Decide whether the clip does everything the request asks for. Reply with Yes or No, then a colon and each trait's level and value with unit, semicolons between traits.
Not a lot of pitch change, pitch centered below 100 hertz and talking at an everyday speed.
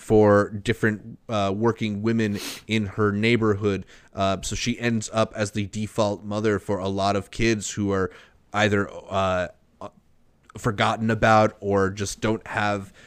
No: narrow, 1.8 semitones; low, 105 Hz; average, 145 wpm